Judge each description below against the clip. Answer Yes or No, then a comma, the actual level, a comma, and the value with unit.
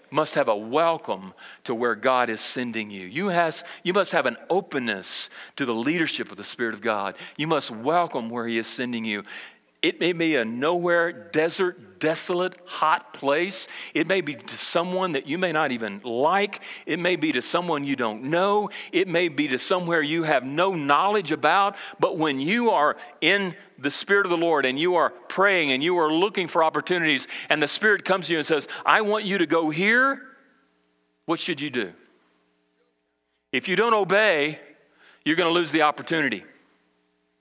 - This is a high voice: No, medium, 165 Hz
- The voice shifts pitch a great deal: Yes, wide, 6.9 semitones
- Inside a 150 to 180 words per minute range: No, average, 190 wpm